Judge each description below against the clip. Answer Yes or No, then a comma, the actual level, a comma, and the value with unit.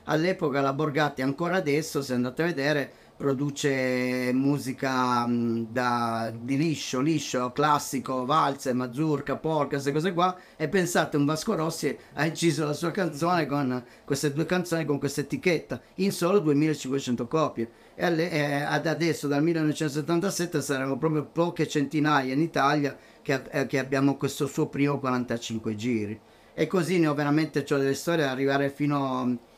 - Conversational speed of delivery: Yes, average, 155 wpm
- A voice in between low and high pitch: Yes, medium, 145 Hz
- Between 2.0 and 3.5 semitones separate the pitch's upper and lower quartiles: Yes, average, 2.9 semitones